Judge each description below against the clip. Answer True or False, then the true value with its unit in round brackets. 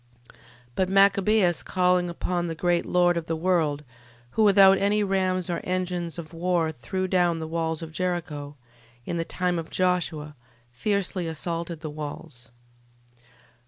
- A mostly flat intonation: True (2.2 semitones)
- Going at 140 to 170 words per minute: True (150 wpm)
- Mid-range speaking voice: True (175 Hz)